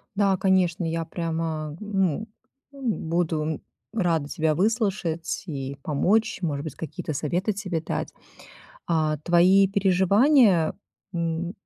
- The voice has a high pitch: No, medium, 170 Hz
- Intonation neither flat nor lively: Yes, average, 3.6 semitones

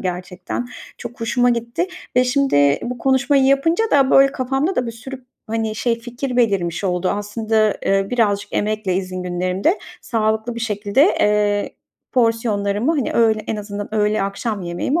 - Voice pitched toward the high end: Yes, high, 225 Hz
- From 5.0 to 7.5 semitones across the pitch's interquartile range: No, average, 3.7 semitones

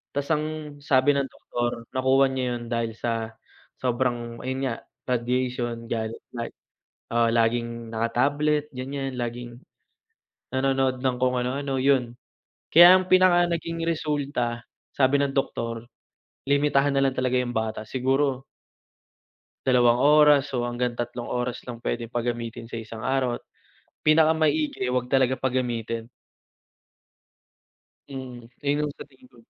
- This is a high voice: No, low, 130 Hz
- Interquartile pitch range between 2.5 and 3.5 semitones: Yes, average, 2.9 semitones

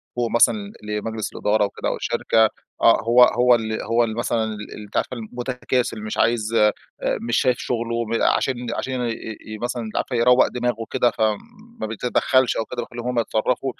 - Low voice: Yes, low, 115 Hz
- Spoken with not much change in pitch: Yes, narrow, 2.0 semitones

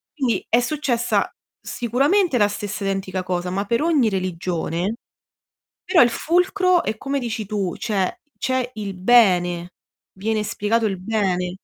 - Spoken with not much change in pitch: No, average, 4.6 semitones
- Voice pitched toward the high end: Yes, high, 215 Hz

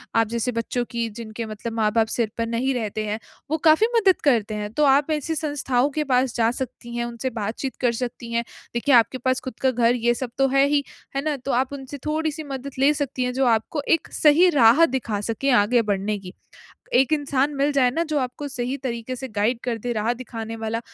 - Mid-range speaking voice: No, very high, 250 Hz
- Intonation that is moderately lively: Yes, average, 3.3 semitones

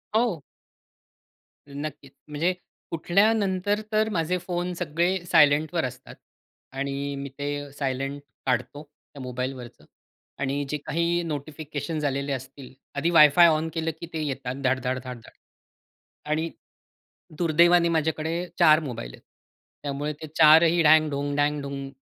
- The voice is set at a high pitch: No, medium, 150 Hz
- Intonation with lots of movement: No, average, 3.3 semitones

